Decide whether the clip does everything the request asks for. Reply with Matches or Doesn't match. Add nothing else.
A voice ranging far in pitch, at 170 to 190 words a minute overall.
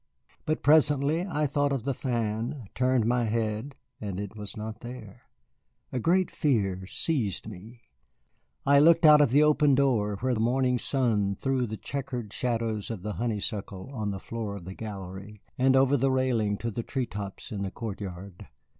Doesn't match